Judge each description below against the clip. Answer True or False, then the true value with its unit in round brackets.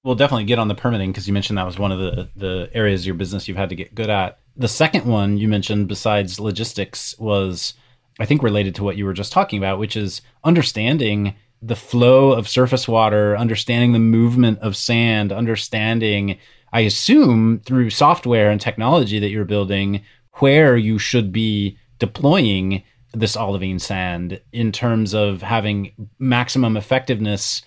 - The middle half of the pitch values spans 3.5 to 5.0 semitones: False (3.1 semitones)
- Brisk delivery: False (175 wpm)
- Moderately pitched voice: False (110 Hz)